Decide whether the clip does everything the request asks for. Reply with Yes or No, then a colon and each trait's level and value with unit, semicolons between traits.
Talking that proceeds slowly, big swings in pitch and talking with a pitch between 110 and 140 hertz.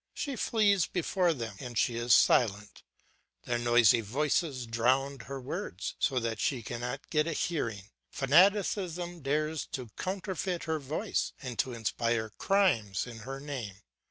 No: average, 145 wpm; wide, 6.1 semitones; low, 135 Hz